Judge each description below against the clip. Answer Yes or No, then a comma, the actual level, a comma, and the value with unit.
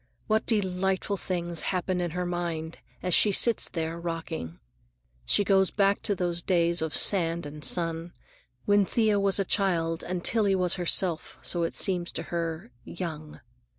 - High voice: No, medium, 175 Hz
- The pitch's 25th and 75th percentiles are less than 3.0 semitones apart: Yes, narrow, 2.6 semitones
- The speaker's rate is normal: Yes, average, 165 wpm